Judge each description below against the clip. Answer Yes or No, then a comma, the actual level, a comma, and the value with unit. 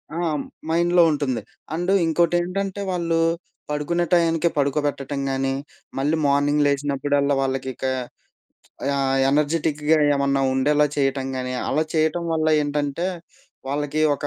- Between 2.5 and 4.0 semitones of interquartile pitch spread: Yes, average, 2.9 semitones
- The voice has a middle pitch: Yes, medium, 145 Hz